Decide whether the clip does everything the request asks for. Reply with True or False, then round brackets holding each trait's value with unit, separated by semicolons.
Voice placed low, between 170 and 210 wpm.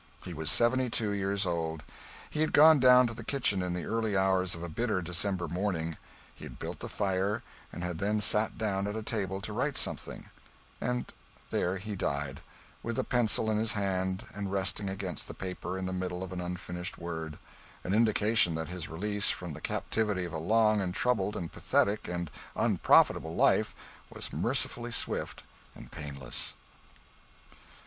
True (95 Hz; 180 wpm)